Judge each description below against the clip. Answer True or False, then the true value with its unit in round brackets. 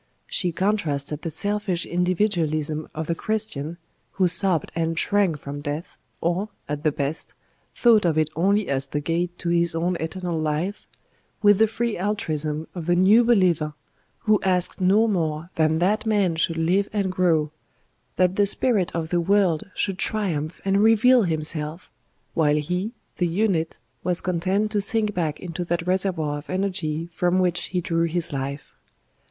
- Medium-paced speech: True (165 wpm)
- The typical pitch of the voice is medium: True (175 Hz)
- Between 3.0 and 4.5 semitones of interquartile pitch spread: True (3.9 semitones)